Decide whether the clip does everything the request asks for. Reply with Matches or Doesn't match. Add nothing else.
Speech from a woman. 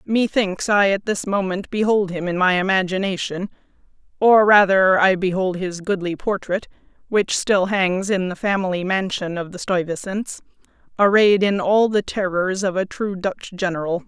Matches